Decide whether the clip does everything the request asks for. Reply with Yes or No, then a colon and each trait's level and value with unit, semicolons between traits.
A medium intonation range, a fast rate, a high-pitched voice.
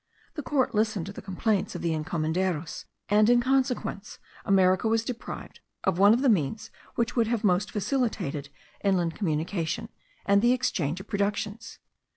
No: average, 4.2 semitones; average, 160 wpm; high, 200 Hz